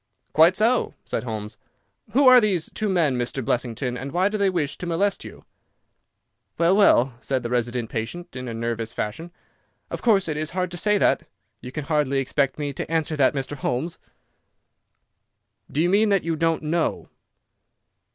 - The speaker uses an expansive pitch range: Yes, wide, 6.2 semitones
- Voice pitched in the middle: Yes, medium, 155 Hz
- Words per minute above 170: Yes, average, 180 wpm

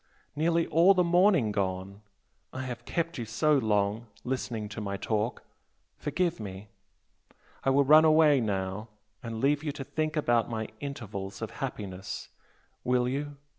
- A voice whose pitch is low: Yes, low, 125 Hz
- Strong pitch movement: Yes, wide, 6.3 semitones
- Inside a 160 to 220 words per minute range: No, average, 150 wpm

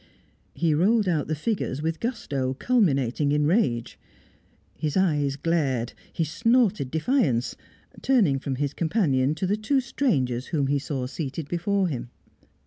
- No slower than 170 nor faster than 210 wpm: No, average, 140 wpm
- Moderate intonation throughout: No, wide, 6.6 semitones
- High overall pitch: No, medium, 155 Hz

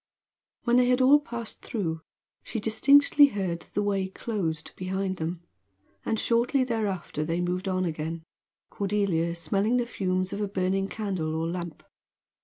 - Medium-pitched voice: No, high, 195 Hz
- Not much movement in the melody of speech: No, average, 4.6 semitones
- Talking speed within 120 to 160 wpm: Yes, average, 150 wpm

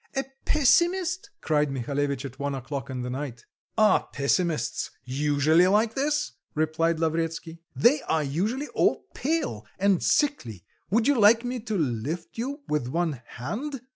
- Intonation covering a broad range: Yes, wide, 9.0 semitones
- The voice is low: No, medium, 165 Hz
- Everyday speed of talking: Yes, average, 145 wpm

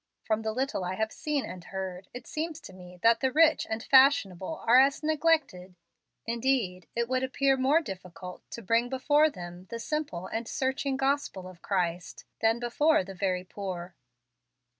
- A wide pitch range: Yes, wide, 6.6 semitones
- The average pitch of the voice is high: Yes, high, 230 Hz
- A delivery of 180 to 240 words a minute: No, average, 170 wpm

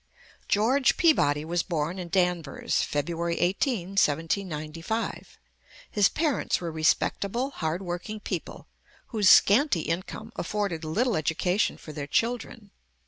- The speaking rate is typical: No, slow, 115 wpm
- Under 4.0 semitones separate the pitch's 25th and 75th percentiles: No, average, 4.8 semitones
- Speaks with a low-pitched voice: No, medium, 180 Hz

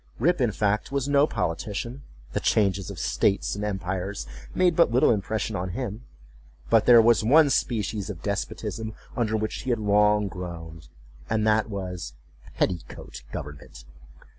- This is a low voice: Yes, low, 105 Hz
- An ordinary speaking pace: Yes, average, 145 wpm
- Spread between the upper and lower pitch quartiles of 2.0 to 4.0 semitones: Yes, average, 3.5 semitones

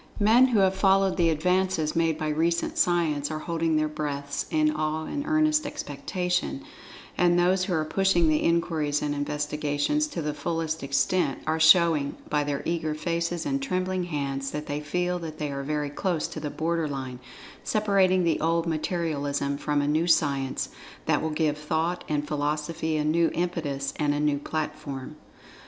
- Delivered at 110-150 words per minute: No, average, 175 wpm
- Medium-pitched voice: Yes, medium, 160 Hz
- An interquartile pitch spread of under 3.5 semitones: Yes, average, 2.9 semitones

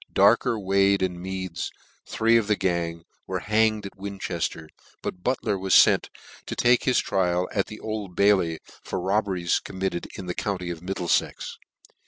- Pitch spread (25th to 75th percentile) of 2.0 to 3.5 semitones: Yes, average, 2.8 semitones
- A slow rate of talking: No, average, 160 wpm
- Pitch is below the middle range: Yes, very low, 95 Hz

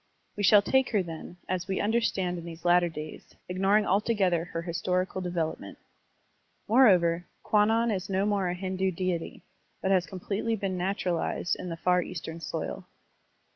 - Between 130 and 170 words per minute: Yes, average, 165 wpm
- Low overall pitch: No, medium, 185 Hz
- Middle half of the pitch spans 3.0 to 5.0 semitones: No, narrow, 2.5 semitones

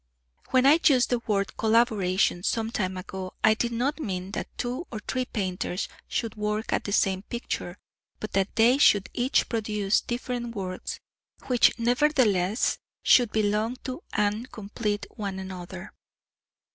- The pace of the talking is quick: No, average, 145 wpm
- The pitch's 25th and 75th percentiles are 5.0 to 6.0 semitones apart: No, average, 3.8 semitones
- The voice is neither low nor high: No, high, 215 Hz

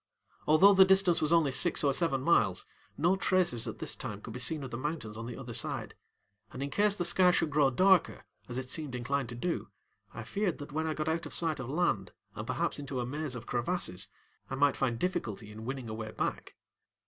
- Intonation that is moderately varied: No, wide, 5.8 semitones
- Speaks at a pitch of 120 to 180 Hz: Yes, medium, 140 Hz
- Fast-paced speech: Yes, fast, 230 wpm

